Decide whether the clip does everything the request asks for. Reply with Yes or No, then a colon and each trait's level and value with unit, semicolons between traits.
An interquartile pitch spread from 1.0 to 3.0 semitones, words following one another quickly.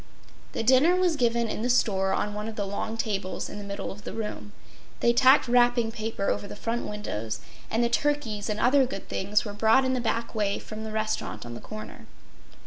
Yes: average, 2.7 semitones; fast, 220 wpm